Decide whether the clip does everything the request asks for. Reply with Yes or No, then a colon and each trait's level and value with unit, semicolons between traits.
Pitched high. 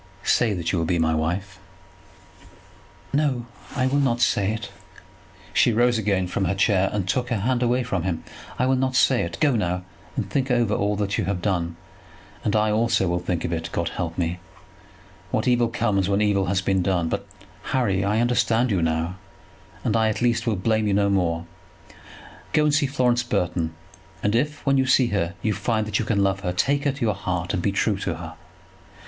No: low, 105 Hz